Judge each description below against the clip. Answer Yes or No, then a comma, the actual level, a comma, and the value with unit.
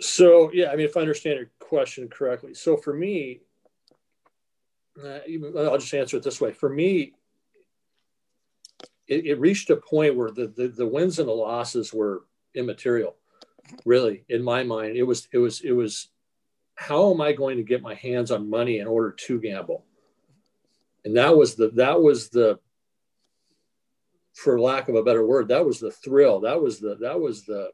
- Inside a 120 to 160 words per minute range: No, average, 185 wpm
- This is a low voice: No, medium, 150 Hz